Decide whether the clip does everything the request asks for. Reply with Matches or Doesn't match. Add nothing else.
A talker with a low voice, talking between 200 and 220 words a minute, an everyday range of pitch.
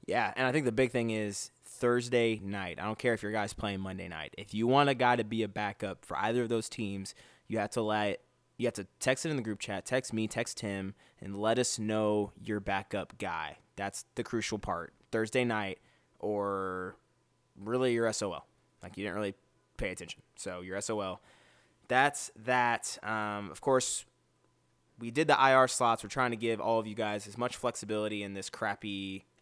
Matches